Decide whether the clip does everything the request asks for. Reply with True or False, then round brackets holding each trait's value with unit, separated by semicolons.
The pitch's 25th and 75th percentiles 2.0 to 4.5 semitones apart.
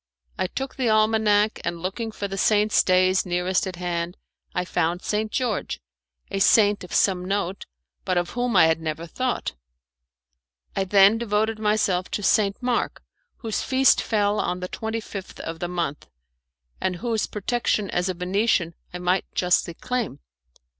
True (3.4 semitones)